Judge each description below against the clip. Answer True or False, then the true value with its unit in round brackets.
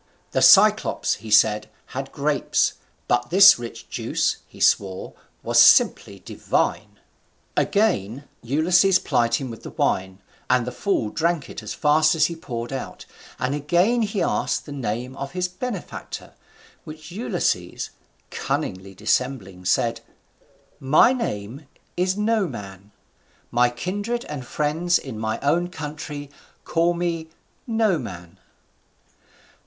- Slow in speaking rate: True (125 wpm)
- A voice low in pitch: False (145 Hz)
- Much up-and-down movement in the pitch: True (7.3 semitones)